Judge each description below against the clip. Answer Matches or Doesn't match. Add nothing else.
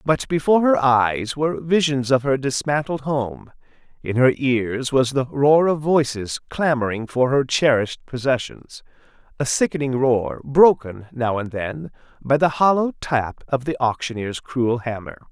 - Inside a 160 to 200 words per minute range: Doesn't match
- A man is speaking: Matches